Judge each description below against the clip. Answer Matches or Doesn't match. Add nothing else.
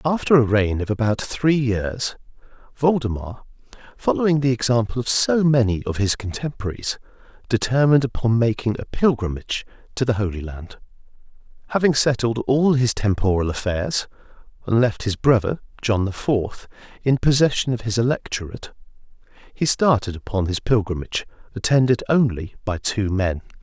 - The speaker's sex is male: Matches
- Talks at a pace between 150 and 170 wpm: Doesn't match